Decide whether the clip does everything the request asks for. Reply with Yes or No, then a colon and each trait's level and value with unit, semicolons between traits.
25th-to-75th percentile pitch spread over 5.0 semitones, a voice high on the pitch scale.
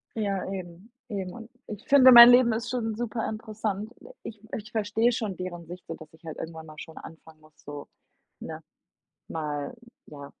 Yes: wide, 5.6 semitones; high, 200 Hz